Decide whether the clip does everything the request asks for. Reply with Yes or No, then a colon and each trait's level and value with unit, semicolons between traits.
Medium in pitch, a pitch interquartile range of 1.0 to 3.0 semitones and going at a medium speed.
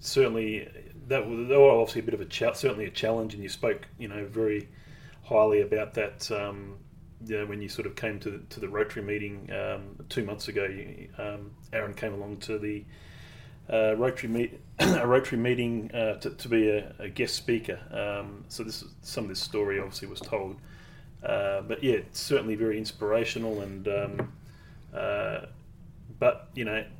No: low, 110 Hz; narrow, 2.4 semitones; average, 185 wpm